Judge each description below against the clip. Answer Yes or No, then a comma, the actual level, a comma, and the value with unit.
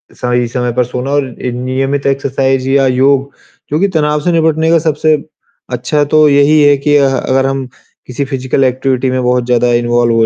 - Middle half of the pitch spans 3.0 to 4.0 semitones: No, narrow, 2.4 semitones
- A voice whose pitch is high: No, low, 135 Hz